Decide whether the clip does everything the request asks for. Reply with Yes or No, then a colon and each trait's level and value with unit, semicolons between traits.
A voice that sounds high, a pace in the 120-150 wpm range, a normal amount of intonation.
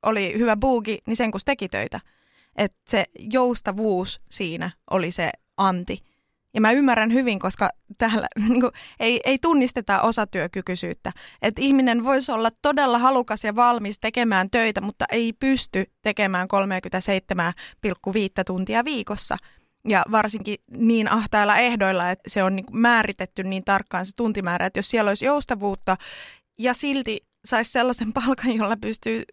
Yes: high, 220 Hz; average, 140 wpm; average, 3.6 semitones